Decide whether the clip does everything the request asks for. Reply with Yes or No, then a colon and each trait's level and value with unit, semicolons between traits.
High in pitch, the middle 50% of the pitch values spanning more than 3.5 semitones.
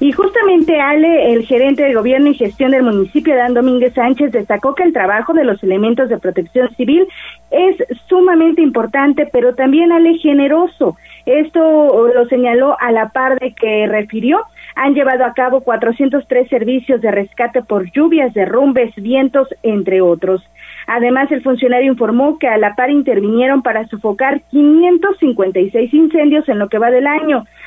Yes: very high, 260 Hz; average, 4.1 semitones